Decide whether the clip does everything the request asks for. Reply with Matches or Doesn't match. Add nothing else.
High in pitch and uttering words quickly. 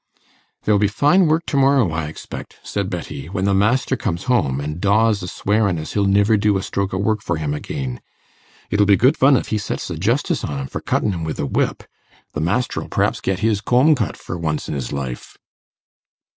Doesn't match